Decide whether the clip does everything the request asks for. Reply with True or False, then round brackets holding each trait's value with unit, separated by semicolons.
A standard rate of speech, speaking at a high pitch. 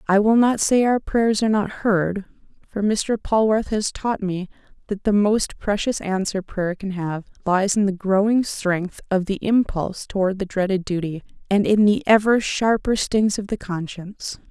True (180 wpm; 200 Hz)